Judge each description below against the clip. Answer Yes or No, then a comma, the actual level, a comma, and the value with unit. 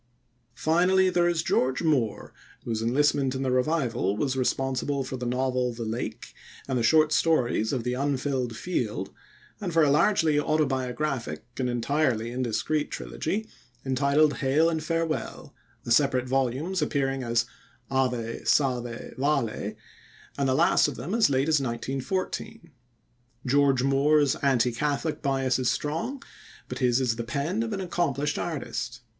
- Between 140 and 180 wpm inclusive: Yes, average, 145 wpm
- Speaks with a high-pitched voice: No, low, 135 Hz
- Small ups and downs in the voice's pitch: No, average, 3.8 semitones